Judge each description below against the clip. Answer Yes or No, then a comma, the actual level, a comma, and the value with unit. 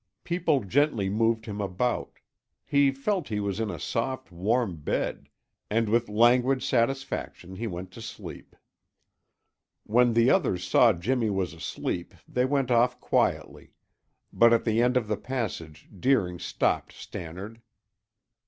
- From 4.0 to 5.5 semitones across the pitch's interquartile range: Yes, average, 4.5 semitones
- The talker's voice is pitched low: Yes, low, 115 Hz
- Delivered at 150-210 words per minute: No, average, 140 wpm